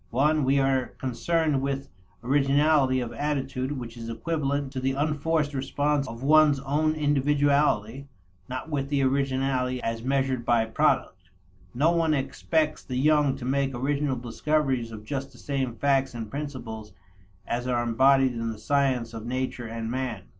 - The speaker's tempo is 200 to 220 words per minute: No, average, 155 wpm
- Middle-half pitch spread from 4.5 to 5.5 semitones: No, average, 2.8 semitones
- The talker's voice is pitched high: No, low, 135 Hz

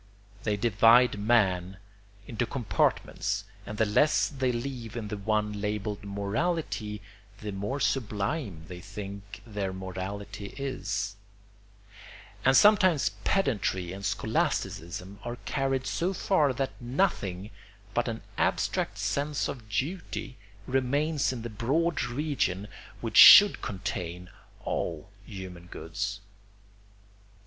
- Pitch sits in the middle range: No, low, 105 Hz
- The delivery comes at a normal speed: No, slow, 110 wpm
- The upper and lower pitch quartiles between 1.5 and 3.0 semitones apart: No, average, 5.1 semitones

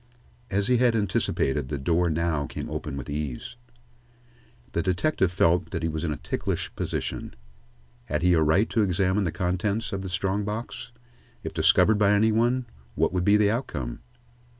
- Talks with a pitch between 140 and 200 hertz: No, very low, 95 Hz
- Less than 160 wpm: No, average, 175 wpm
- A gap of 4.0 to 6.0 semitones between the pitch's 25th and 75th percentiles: Yes, average, 4.6 semitones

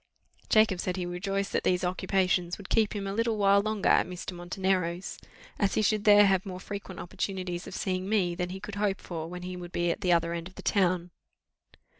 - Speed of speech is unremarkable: No, fast, 220 wpm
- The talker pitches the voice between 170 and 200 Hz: Yes, medium, 185 Hz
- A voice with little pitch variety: Yes, narrow, 2.1 semitones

